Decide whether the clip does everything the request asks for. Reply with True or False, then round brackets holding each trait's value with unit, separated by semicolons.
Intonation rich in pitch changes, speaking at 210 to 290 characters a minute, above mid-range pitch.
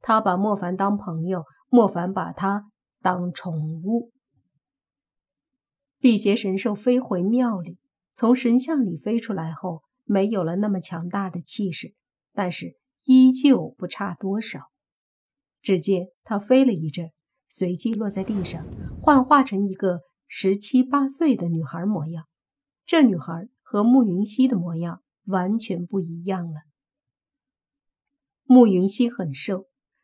False (5.7 semitones; 190 characters per minute; 200 Hz)